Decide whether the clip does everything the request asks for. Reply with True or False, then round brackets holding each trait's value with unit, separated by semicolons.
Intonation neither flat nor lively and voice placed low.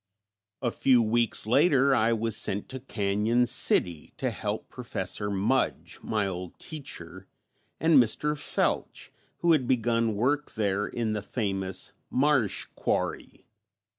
True (4.4 semitones; 115 Hz)